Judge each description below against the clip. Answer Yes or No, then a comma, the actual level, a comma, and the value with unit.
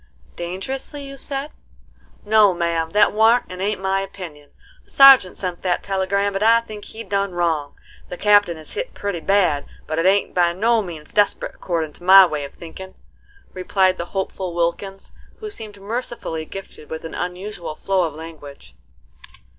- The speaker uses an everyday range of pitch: Yes, average, 3.4 semitones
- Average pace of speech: Yes, average, 170 wpm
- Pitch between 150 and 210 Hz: Yes, high, 190 Hz